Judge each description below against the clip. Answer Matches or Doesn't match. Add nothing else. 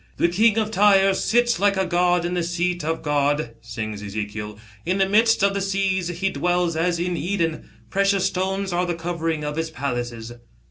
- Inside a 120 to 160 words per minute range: Doesn't match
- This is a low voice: Doesn't match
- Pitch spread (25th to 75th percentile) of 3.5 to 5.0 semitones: Matches